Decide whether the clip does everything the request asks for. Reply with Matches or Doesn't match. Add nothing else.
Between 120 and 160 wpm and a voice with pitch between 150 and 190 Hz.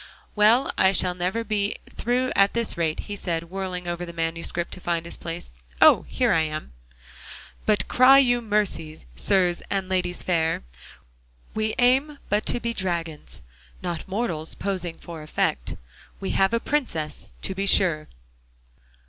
Matches